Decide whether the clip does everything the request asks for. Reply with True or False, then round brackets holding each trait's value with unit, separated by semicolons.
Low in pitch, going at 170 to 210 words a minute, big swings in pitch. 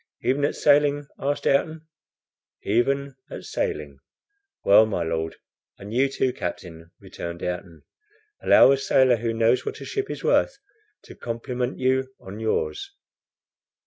False (125 Hz; 140 wpm; 5.8 semitones)